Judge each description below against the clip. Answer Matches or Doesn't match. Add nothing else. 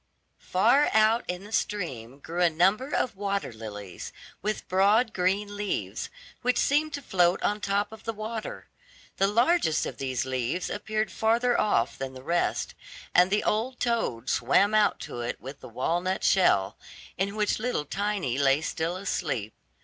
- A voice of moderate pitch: Doesn't match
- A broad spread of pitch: Matches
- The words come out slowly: Doesn't match